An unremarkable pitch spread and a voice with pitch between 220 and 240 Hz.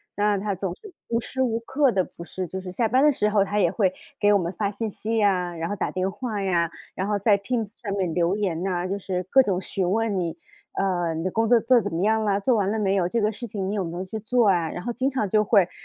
No: average, 3.1 semitones; high, 200 Hz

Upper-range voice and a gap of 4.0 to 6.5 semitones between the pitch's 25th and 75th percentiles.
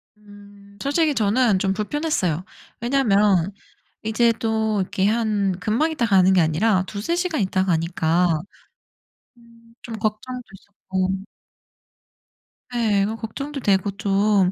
No: high, 210 Hz; average, 3.4 semitones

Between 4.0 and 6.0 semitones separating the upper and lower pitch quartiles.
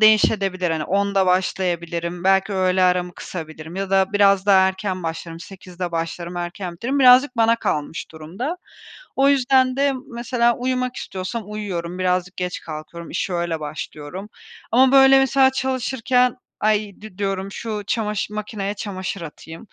Yes: average, 4.7 semitones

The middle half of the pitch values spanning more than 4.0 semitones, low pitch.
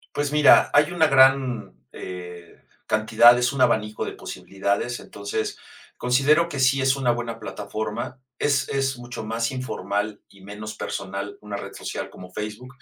Yes: average, 4.4 semitones; low, 120 Hz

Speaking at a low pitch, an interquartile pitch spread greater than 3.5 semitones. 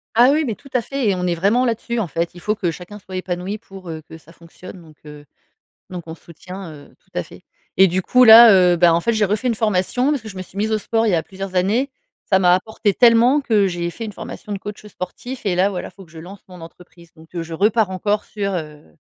No: high, 190 Hz; average, 4.0 semitones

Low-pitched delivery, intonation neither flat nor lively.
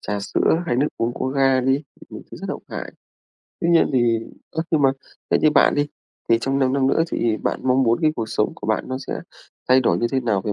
Yes: low, 130 Hz; average, 3.2 semitones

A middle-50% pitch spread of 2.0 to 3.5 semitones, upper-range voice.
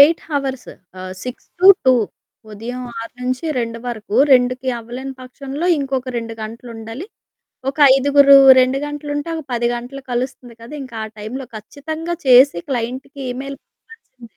Yes: average, 2.8 semitones; very high, 255 Hz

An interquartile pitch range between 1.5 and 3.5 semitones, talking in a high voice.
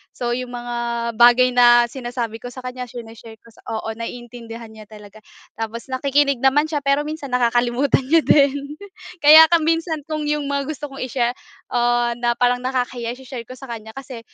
Yes: average, 2.8 semitones; very high, 250 Hz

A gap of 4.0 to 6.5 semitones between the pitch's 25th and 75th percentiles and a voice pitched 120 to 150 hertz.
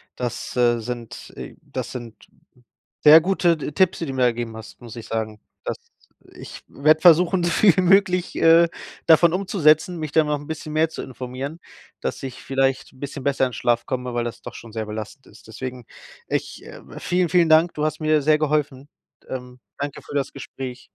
Yes: average, 4.6 semitones; medium, 140 Hz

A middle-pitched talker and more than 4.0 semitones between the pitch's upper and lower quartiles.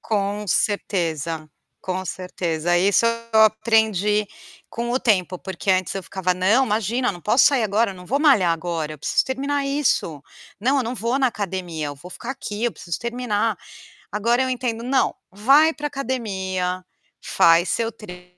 No: high, 210 Hz; average, 4.8 semitones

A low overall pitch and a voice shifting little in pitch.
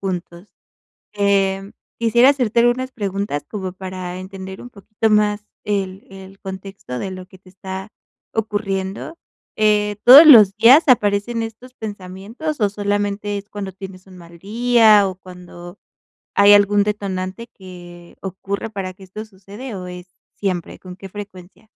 No: high, 200 Hz; narrow, 2.2 semitones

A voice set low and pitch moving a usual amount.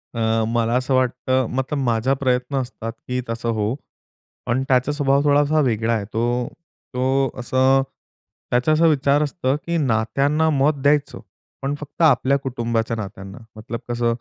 Yes: low, 130 Hz; average, 3.2 semitones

